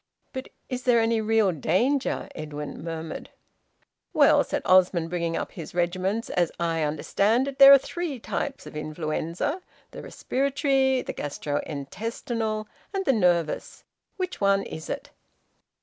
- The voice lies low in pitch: No, high, 200 Hz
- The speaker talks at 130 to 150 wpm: Yes, average, 140 wpm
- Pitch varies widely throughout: Yes, wide, 7.8 semitones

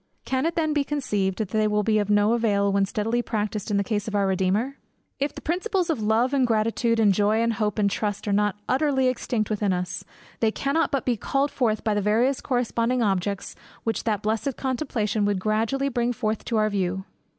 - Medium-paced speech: No, fast, 215 wpm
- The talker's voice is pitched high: Yes, high, 220 Hz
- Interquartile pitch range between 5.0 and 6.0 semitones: No, average, 3.5 semitones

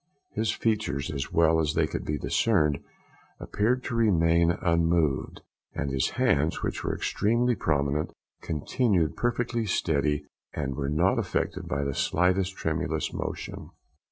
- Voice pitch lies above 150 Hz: No, very low, 80 Hz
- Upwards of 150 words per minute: No, slow, 135 wpm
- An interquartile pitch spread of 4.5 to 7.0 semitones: Yes, wide, 5.6 semitones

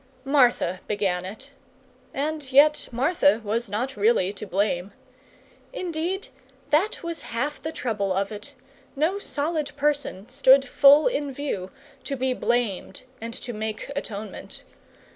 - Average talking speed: No, slow, 130 wpm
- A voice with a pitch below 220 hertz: No, very high, 260 Hz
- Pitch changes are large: Yes, wide, 5.8 semitones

